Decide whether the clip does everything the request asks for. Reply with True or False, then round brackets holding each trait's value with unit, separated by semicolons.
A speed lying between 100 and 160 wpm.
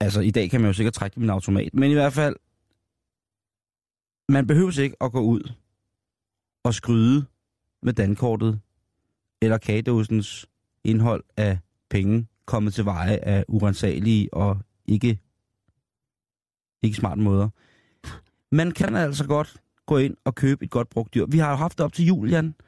True (155 wpm)